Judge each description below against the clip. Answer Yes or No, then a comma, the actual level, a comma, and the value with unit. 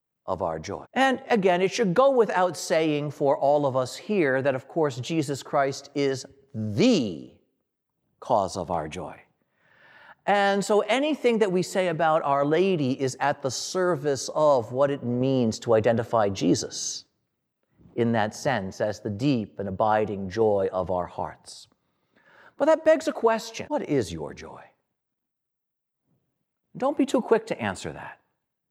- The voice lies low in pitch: No, medium, 145 Hz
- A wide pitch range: Yes, wide, 8.0 semitones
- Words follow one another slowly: No, average, 155 wpm